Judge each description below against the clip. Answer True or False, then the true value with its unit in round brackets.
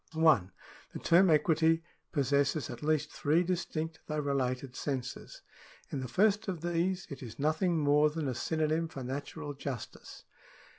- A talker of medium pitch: True (155 Hz)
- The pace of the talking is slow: False (150 wpm)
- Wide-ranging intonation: False (2.9 semitones)